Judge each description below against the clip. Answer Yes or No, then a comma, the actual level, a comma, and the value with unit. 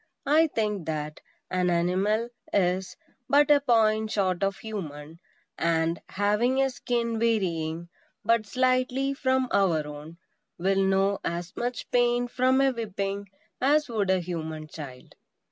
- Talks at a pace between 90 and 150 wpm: Yes, slow, 135 wpm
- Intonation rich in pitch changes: Yes, wide, 6.0 semitones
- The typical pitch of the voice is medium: No, high, 200 Hz